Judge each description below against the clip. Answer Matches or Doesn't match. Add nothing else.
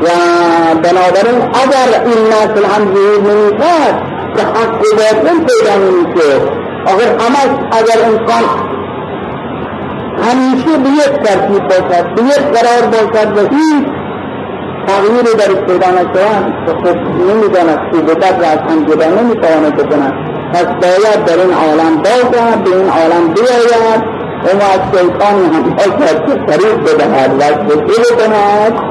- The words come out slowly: Matches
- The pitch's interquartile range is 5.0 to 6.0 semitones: Doesn't match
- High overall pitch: Matches